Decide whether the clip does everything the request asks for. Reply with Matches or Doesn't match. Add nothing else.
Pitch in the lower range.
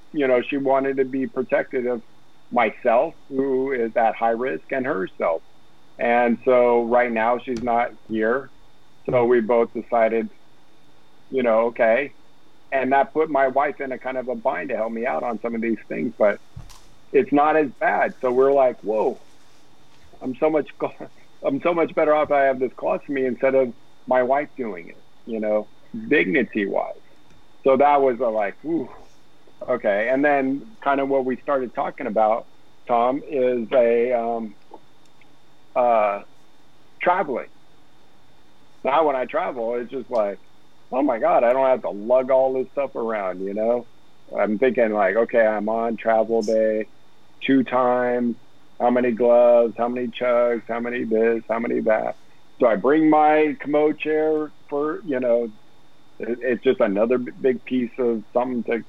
Matches